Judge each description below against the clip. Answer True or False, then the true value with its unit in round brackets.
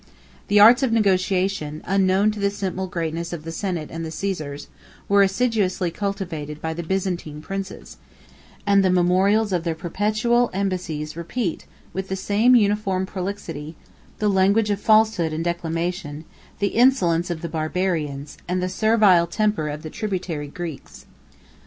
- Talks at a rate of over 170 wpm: False (150 wpm)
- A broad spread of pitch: False (3.6 semitones)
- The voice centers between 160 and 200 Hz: True (185 Hz)